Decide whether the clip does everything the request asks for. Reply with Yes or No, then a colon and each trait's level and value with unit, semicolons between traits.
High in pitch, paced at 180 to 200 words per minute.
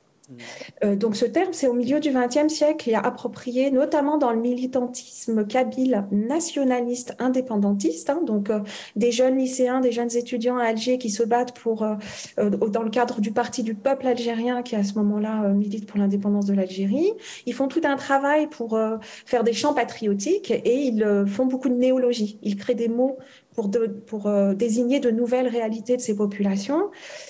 Yes: high, 245 Hz; average, 195 wpm